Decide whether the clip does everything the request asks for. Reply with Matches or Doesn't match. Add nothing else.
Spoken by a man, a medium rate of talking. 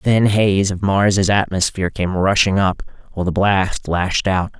Matches